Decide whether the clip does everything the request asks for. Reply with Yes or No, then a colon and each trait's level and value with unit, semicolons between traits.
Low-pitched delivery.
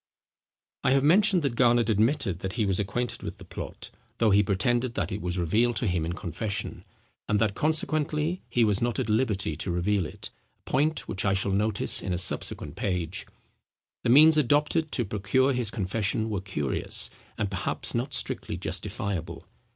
Yes: low, 110 Hz